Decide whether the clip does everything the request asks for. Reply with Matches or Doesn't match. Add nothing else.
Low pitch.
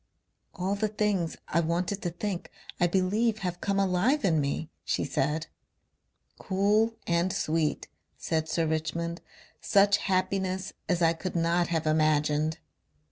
Doesn't match